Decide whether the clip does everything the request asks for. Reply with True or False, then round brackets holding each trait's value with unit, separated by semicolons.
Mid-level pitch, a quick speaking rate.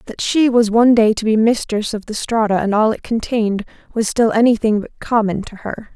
False (220 Hz; 220 wpm)